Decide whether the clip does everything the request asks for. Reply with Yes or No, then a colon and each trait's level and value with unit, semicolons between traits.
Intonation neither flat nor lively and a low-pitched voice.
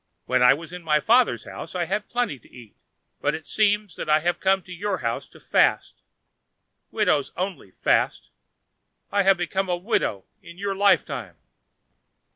No: average, 4.7 semitones; medium, 180 Hz